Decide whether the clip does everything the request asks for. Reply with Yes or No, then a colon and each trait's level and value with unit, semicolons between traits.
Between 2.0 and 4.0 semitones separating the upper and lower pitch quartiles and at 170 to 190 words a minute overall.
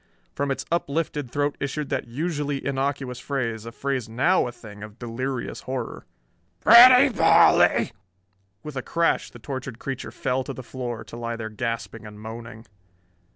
No: average, 3.5 semitones; average, 155 wpm